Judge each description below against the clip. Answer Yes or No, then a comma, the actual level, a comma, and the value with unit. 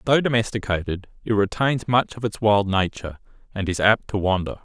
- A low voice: Yes, low, 105 Hz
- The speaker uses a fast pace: No, average, 180 wpm